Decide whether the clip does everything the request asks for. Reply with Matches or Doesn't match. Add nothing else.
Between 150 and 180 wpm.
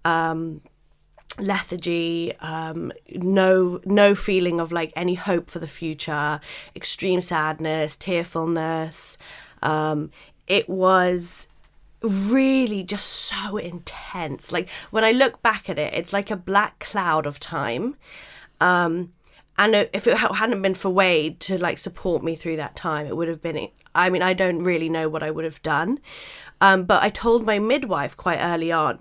Matches